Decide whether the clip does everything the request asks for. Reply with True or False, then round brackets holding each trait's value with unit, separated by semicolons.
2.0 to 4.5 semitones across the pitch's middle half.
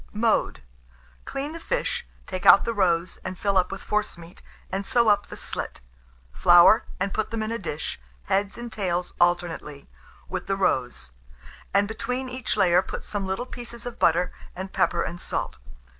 True (4.2 semitones)